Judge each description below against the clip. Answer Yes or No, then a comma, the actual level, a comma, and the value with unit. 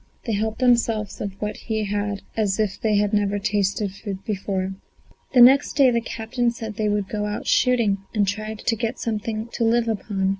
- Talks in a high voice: Yes, high, 215 Hz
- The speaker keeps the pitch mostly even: Yes, narrow, 2.1 semitones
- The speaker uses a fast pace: Yes, fast, 210 wpm